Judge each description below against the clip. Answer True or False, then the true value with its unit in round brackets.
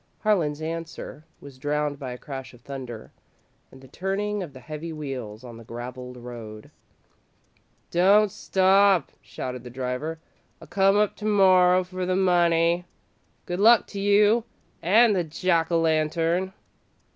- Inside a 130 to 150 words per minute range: True (145 wpm)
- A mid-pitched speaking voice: True (165 Hz)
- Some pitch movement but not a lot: False (6.2 semitones)